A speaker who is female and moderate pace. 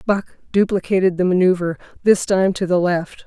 Yes: female; average, 165 wpm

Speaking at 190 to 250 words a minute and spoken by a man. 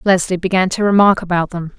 No: average, 200 wpm; female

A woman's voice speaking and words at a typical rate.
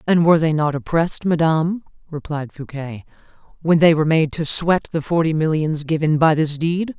Yes: female; average, 180 wpm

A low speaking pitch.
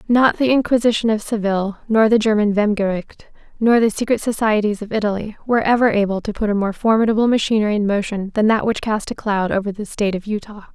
No: high, 215 Hz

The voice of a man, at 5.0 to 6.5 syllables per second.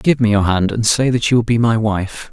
Yes: male; 5.3 syllables/s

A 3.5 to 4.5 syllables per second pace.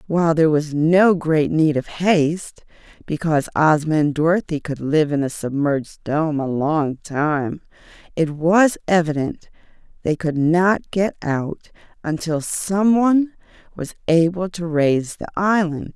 Yes: 4.2 syllables/s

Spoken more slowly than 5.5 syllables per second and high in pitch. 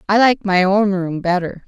Yes: 4.7 syllables/s; high, 195 Hz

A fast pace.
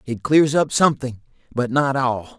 No: average, 175 wpm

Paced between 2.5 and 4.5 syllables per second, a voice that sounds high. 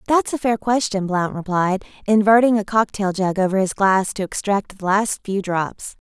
No: 4.7 syllables/s; high, 205 Hz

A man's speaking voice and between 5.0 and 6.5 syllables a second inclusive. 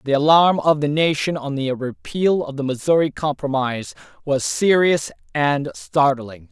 No: male; 4.5 syllables/s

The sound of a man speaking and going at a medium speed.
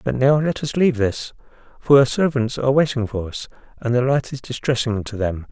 No: male; fast, 220 wpm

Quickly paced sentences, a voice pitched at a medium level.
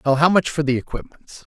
Yes: fast, 235 wpm; medium, 150 Hz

